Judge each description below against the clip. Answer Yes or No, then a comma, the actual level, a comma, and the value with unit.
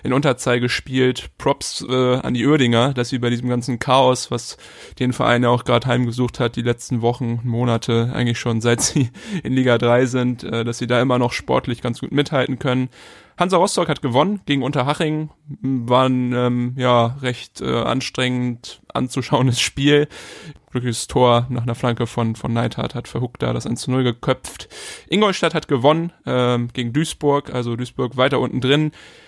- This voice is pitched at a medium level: No, low, 125 Hz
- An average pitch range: No, narrow, 2.1 semitones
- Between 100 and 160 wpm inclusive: No, average, 170 wpm